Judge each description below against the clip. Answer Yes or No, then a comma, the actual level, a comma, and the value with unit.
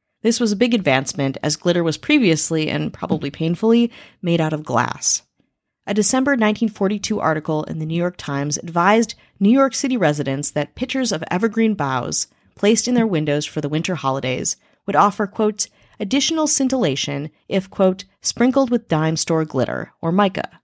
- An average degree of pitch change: No, wide, 6.5 semitones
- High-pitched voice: Yes, high, 195 Hz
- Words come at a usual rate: Yes, average, 165 wpm